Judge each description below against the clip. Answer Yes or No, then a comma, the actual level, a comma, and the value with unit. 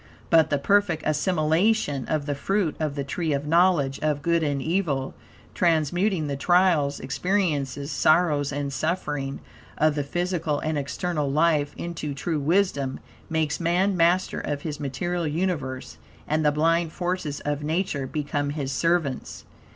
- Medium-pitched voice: Yes, medium, 155 Hz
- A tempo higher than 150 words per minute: No, average, 145 wpm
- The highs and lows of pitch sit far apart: No, average, 3.3 semitones